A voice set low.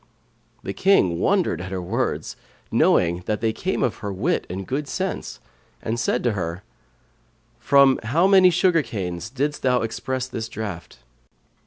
Yes: low, 115 Hz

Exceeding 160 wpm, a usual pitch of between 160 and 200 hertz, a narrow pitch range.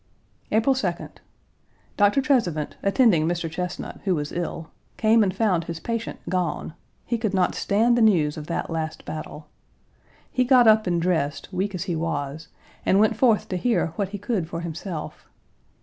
No: average, 170 wpm; medium, 185 Hz; average, 5.0 semitones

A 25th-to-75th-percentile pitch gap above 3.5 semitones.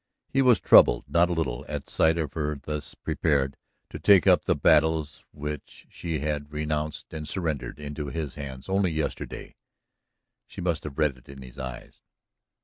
No: narrow, 2.4 semitones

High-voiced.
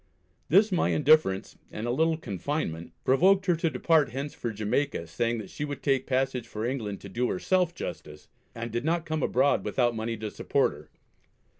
No: low, 130 Hz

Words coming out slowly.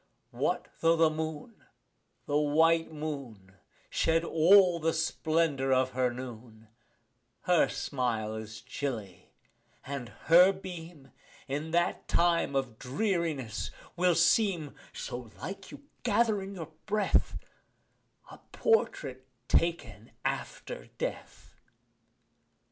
Yes: slow, 105 wpm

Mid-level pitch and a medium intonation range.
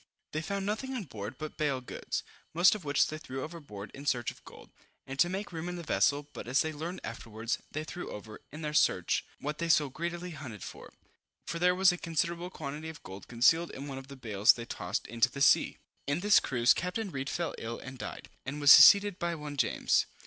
Yes: medium, 150 Hz; average, 4.7 semitones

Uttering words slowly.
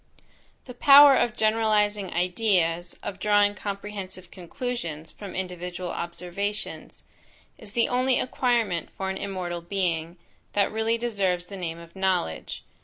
Yes: slow, 125 wpm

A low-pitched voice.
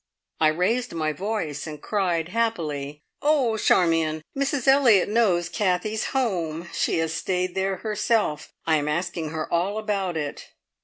No: medium, 180 Hz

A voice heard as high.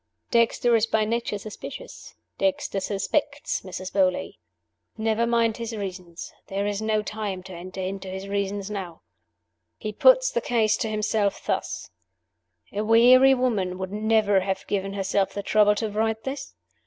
Yes: high, 210 Hz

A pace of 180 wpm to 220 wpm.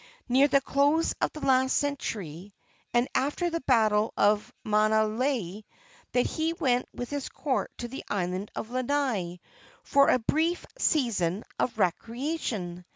No: average, 140 wpm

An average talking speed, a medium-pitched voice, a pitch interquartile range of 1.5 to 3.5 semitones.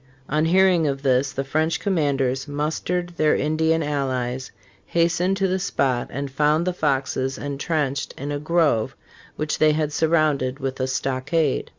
Yes: average, 155 wpm; medium, 150 Hz; average, 3.2 semitones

